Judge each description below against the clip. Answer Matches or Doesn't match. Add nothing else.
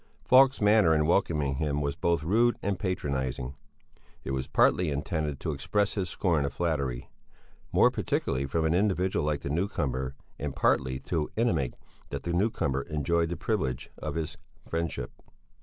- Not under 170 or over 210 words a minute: Doesn't match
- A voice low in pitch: Matches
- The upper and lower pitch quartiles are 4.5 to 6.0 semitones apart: Matches